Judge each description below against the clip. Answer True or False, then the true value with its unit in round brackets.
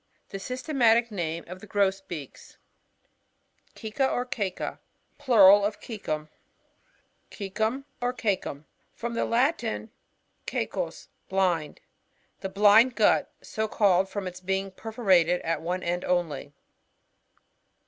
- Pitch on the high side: True (200 Hz)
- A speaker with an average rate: False (115 wpm)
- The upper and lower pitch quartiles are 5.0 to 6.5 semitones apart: False (4.1 semitones)